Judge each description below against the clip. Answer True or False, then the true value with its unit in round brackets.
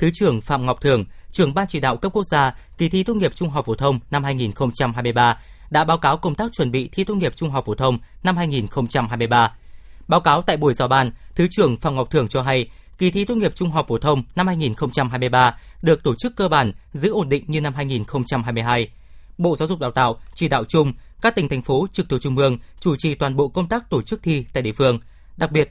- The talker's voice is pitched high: False (145 Hz)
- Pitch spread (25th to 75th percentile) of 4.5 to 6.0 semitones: True (5.3 semitones)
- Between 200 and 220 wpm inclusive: False (240 wpm)